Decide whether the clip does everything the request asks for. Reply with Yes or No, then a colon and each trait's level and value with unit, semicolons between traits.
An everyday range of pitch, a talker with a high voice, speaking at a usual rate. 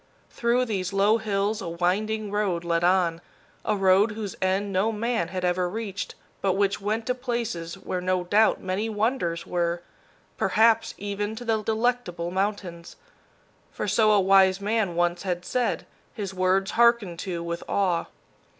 Yes: average, 3.4 semitones; high, 195 Hz; average, 160 wpm